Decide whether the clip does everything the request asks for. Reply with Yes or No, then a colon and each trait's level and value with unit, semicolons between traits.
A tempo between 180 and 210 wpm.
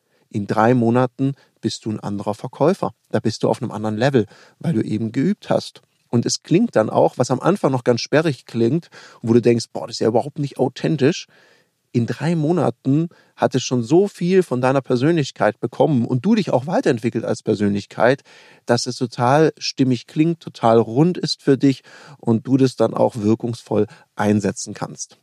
Yes: fast, 190 wpm